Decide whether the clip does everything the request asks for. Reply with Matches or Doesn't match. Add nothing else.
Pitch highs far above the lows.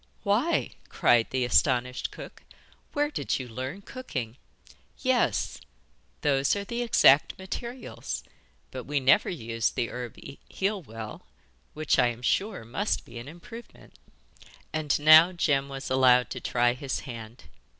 Matches